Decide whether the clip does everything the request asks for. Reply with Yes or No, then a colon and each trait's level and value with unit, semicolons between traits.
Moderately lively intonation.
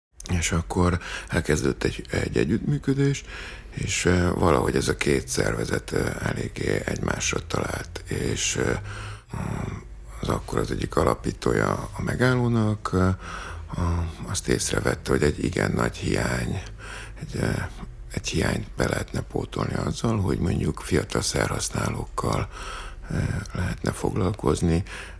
Yes: average, 4.1 semitones